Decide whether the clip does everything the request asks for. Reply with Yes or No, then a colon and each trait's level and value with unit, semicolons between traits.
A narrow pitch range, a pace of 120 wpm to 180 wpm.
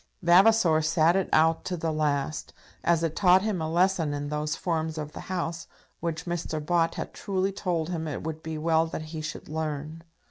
No: narrow, 1.9 semitones; average, 200 wpm